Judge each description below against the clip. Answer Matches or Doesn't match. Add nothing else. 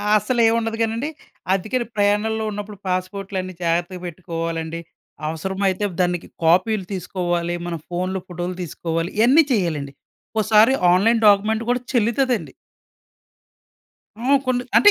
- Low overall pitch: Doesn't match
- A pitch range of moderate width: Matches